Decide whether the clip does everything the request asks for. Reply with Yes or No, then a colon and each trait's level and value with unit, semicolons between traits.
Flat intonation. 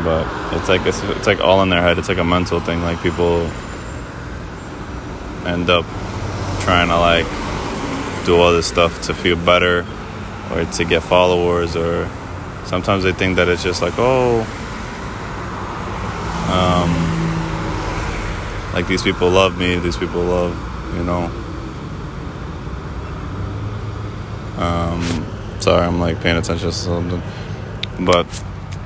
Yes: narrow, 2.3 semitones